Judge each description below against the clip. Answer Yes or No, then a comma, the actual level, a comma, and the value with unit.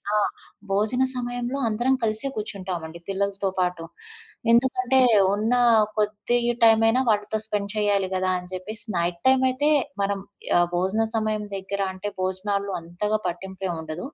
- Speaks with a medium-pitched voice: No, high, 205 Hz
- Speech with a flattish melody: No, average, 3.0 semitones